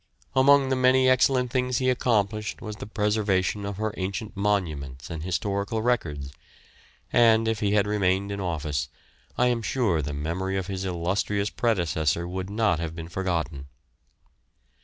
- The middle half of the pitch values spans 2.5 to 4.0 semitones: No, average, 4.7 semitones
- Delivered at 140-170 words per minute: Yes, average, 155 wpm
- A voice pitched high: No, low, 100 Hz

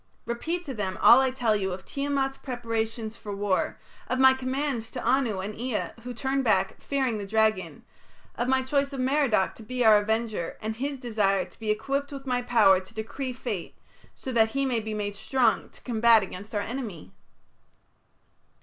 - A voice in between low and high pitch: No, high, 235 Hz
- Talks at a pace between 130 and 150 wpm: No, average, 185 wpm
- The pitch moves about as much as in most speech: Yes, average, 3.7 semitones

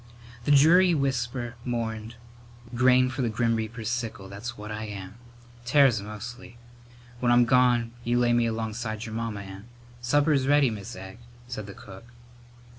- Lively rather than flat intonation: No, narrow, 2.4 semitones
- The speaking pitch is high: No, low, 120 Hz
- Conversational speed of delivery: Yes, average, 160 wpm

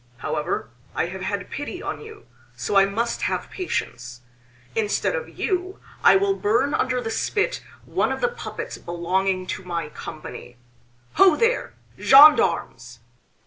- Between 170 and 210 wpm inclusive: No, average, 145 wpm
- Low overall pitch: No, high, 215 Hz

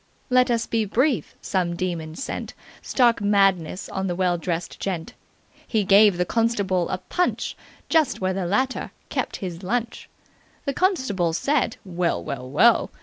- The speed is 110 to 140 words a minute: No, average, 150 wpm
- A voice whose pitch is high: Yes, high, 195 Hz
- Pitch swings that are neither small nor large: Yes, average, 5.0 semitones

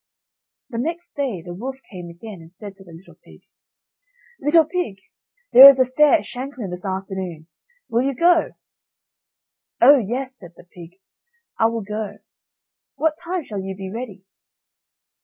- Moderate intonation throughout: No, wide, 6.4 semitones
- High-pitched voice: Yes, high, 225 Hz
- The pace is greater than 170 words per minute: No, average, 160 wpm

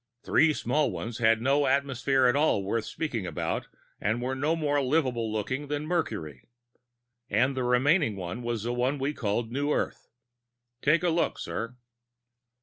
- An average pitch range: Yes, average, 4.4 semitones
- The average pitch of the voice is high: No, low, 130 Hz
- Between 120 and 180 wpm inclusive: Yes, average, 160 wpm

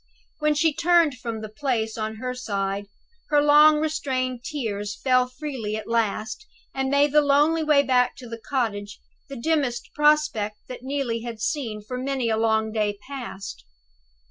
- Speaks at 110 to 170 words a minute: Yes, average, 165 wpm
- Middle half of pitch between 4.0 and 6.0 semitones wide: Yes, average, 4.9 semitones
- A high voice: Yes, very high, 250 Hz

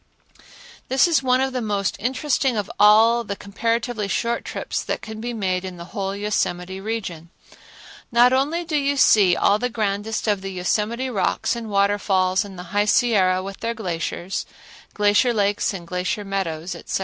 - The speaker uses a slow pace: No, average, 175 wpm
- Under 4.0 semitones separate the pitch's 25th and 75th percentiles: Yes, average, 3.6 semitones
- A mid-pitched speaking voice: No, high, 210 Hz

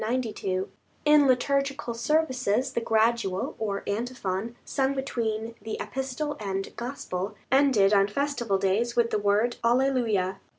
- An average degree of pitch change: Yes, average, 4.7 semitones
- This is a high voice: Yes, high, 235 Hz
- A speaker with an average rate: No, slow, 120 wpm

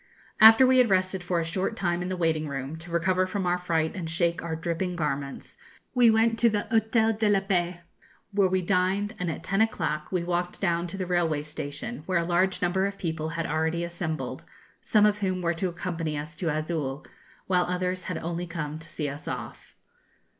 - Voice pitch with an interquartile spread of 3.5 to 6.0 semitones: No, average, 2.9 semitones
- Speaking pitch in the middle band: Yes, medium, 175 Hz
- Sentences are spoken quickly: Yes, fast, 210 wpm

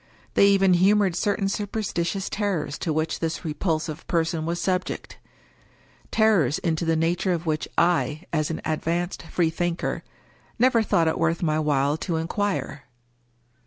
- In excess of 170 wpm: No, average, 150 wpm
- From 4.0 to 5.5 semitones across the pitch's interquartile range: No, average, 3.3 semitones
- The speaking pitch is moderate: Yes, medium, 170 Hz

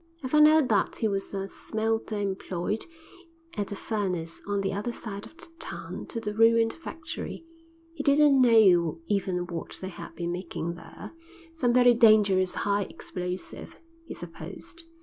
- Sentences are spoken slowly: No, average, 160 wpm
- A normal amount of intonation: Yes, average, 4.2 semitones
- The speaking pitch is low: No, high, 205 Hz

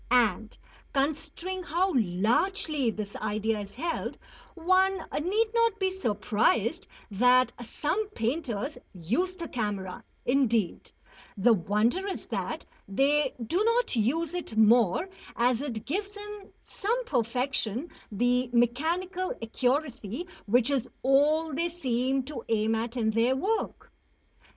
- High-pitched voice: Yes, very high, 260 Hz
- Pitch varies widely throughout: Yes, wide, 7.5 semitones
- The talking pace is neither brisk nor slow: No, slow, 120 wpm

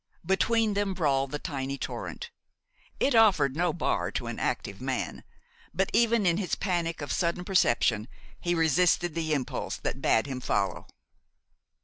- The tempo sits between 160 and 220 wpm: No, average, 150 wpm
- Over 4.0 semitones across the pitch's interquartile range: Yes, wide, 5.5 semitones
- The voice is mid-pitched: Yes, medium, 170 Hz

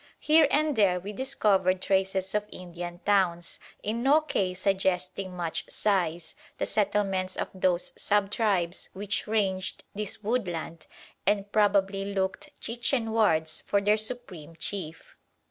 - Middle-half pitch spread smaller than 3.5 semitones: Yes, narrow, 2.6 semitones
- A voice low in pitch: No, high, 195 Hz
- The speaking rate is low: Yes, slow, 130 wpm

